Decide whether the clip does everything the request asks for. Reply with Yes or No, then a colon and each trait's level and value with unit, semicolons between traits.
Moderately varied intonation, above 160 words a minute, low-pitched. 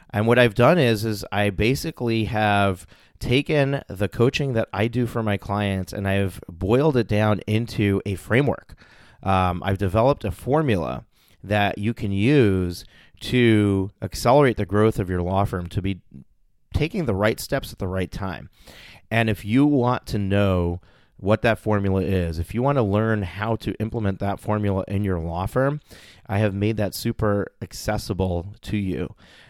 Yes: average, 3.2 semitones; average, 175 wpm; low, 105 Hz